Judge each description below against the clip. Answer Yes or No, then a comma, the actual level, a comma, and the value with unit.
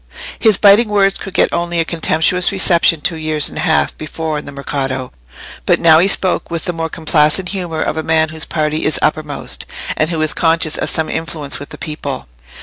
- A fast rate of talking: Yes, fast, 210 wpm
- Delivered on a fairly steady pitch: Yes, narrow, 2.1 semitones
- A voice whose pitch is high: No, medium, 160 Hz